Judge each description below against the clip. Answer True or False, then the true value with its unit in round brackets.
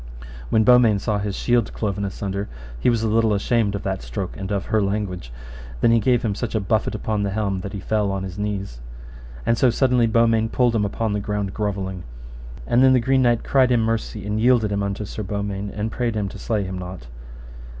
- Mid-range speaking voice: False (105 Hz)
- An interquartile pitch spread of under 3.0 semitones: True (2.5 semitones)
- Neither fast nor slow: False (225 wpm)